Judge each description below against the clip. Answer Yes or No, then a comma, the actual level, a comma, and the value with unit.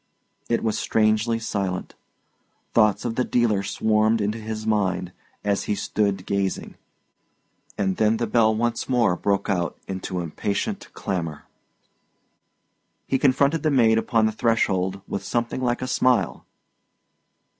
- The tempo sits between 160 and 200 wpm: No, slow, 135 wpm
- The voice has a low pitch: Yes, low, 110 Hz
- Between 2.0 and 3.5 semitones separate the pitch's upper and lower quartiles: Yes, average, 2.9 semitones